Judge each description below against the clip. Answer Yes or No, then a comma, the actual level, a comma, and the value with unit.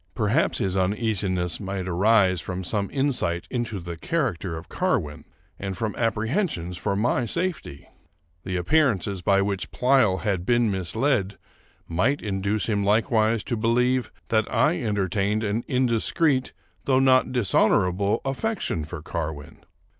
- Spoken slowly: Yes, slow, 130 wpm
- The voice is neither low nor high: No, low, 105 Hz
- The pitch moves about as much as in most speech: Yes, average, 4.8 semitones